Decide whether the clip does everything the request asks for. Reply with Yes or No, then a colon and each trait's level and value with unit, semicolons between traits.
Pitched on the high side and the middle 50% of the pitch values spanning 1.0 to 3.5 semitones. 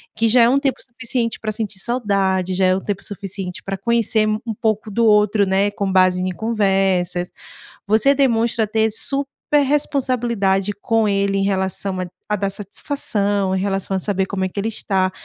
Yes: high, 205 Hz; average, 3.0 semitones